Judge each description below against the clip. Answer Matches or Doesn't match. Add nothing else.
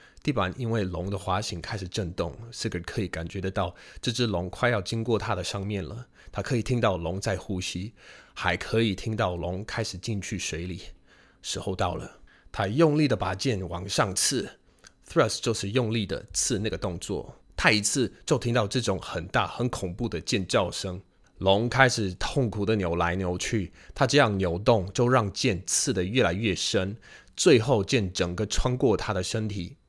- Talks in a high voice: Doesn't match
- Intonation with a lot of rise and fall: Doesn't match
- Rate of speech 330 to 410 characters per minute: Doesn't match